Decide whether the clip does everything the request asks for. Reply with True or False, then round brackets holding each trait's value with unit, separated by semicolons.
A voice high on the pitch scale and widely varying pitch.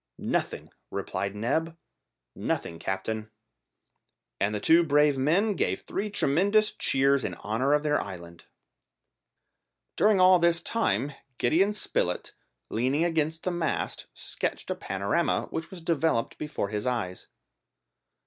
False (150 Hz; 7.6 semitones)